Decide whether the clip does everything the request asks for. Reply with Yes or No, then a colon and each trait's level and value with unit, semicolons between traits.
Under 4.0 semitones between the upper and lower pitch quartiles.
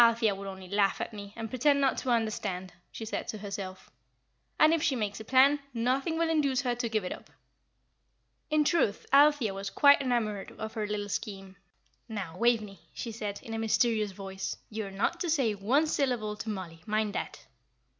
No: average, 4.4 semitones